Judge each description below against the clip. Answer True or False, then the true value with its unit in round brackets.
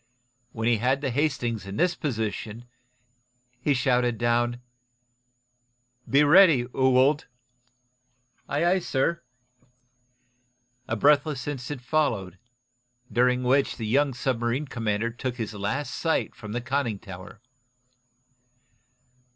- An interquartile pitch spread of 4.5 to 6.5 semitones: False (3.7 semitones)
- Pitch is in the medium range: False (125 Hz)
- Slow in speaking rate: True (110 wpm)